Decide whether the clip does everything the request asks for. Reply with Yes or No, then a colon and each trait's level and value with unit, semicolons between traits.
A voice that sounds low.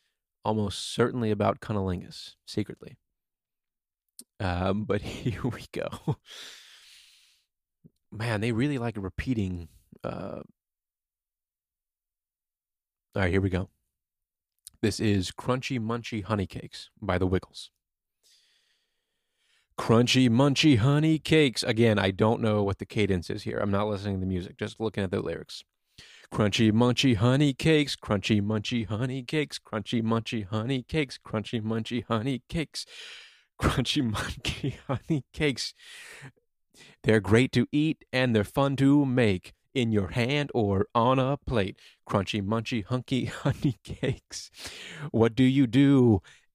Yes: low, 115 Hz